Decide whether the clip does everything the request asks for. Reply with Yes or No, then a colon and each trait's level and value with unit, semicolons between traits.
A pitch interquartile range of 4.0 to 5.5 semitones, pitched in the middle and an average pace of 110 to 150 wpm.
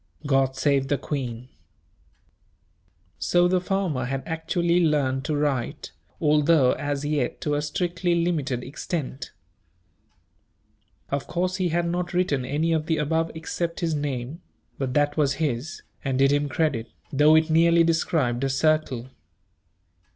No: average, 3.6 semitones; medium, 150 Hz; average, 140 wpm